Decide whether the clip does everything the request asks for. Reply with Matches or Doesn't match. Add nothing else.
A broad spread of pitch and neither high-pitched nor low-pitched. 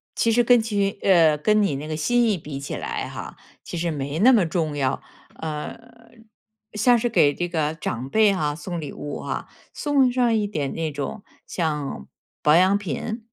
Matches